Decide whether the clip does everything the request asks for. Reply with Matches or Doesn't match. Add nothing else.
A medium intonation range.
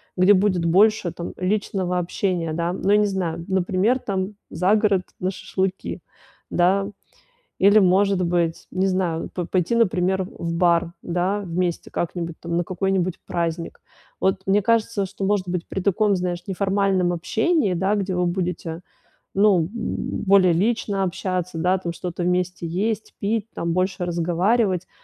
Doesn't match